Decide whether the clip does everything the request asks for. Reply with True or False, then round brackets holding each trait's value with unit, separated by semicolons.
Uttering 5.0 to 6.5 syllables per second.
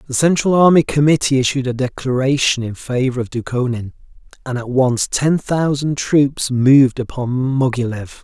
False (4.8 syllables/s)